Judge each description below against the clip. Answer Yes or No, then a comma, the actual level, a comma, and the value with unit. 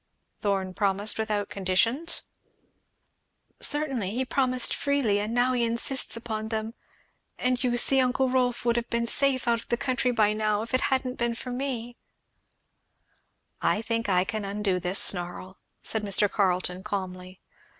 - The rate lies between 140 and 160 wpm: Yes, average, 155 wpm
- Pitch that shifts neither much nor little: Yes, average, 3.9 semitones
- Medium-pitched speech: No, high, 230 Hz